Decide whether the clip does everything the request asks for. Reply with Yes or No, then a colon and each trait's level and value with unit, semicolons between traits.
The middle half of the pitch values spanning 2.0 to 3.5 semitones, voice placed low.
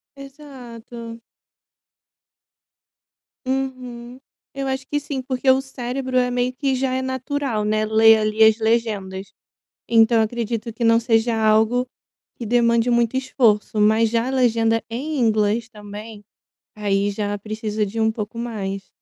No: average, 2.8 semitones; high, 230 Hz